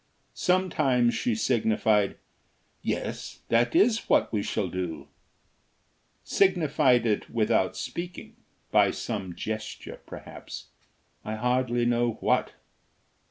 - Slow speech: Yes, slow, 100 wpm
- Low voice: Yes, low, 120 Hz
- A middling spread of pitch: Yes, average, 4.2 semitones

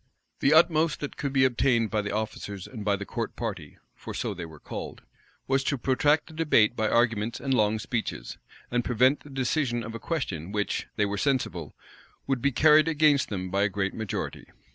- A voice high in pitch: No, low, 120 Hz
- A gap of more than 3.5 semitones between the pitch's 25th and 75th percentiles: Yes, average, 5.1 semitones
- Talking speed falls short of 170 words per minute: No, average, 200 wpm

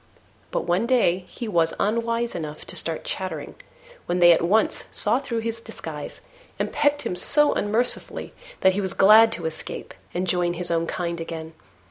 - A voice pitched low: No, medium, 185 Hz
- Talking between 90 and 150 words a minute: No, average, 175 wpm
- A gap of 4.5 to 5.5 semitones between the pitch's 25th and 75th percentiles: Yes, average, 5.0 semitones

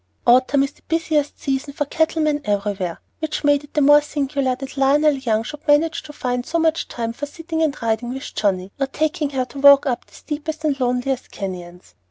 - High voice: Yes, very high, 280 Hz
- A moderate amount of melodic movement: Yes, average, 3.4 semitones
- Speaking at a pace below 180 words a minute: No, fast, 205 wpm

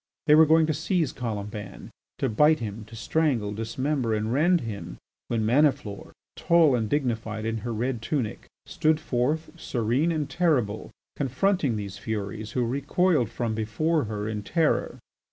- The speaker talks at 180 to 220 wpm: No, average, 155 wpm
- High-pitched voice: No, low, 120 Hz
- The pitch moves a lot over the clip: Yes, wide, 5.9 semitones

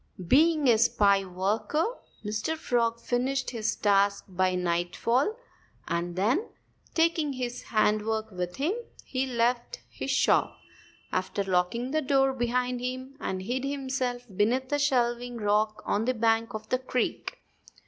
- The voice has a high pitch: Yes, high, 240 Hz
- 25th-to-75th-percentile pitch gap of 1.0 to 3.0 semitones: No, average, 4.1 semitones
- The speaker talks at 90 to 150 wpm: Yes, average, 140 wpm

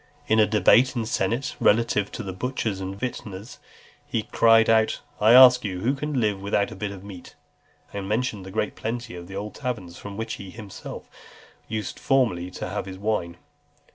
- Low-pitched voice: Yes, low, 105 Hz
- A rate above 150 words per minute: Yes, average, 190 wpm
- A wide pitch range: No, average, 3.2 semitones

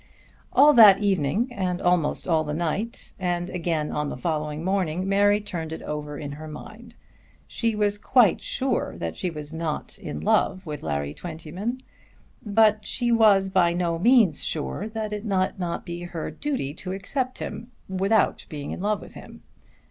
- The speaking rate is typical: Yes, average, 170 wpm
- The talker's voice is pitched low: No, medium, 185 Hz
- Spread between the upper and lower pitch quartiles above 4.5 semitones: Yes, average, 5.1 semitones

